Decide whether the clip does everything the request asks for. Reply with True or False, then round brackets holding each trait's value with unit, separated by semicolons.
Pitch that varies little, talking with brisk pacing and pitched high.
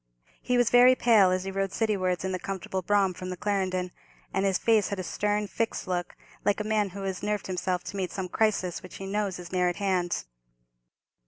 True (2.2 semitones; 220 wpm; 195 Hz)